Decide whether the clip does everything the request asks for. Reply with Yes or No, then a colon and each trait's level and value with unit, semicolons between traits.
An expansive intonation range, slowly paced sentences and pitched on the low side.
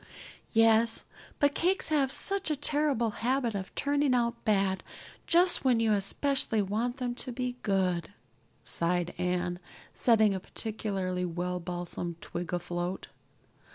No: wide, 6.0 semitones; slow, 130 wpm; high, 220 Hz